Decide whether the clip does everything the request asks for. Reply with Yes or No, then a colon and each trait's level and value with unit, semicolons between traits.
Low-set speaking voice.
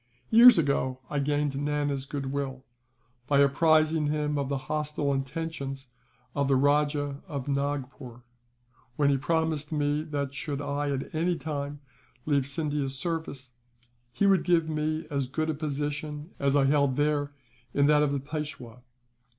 No: medium, 145 Hz